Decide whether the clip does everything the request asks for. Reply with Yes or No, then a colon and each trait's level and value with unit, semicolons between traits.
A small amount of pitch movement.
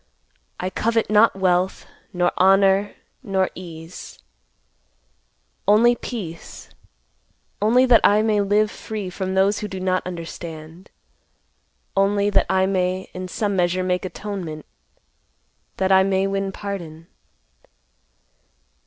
Yes: narrow, 2.1 semitones